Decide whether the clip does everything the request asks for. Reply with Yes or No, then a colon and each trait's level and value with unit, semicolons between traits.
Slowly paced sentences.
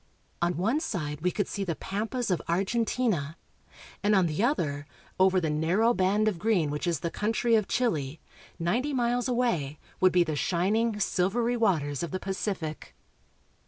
No: average, 165 wpm